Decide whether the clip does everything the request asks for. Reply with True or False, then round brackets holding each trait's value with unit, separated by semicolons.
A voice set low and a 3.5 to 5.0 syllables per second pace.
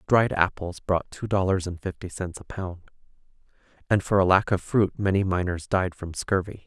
True (95 Hz; 4.8 syllables/s)